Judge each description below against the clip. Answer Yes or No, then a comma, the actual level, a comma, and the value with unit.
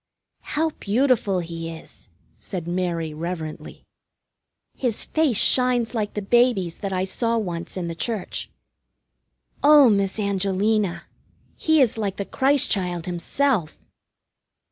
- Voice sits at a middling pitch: No, high, 200 Hz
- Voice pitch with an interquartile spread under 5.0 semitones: No, wide, 5.5 semitones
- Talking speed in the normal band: No, slow, 120 wpm